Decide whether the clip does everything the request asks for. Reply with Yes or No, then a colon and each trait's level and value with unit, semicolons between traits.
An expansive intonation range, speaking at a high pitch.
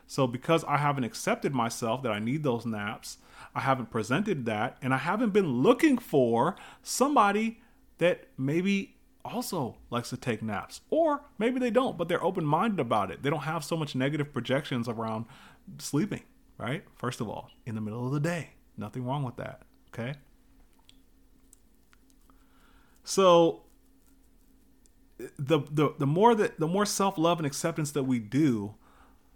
No: wide, 8.1 semitones; medium, 150 Hz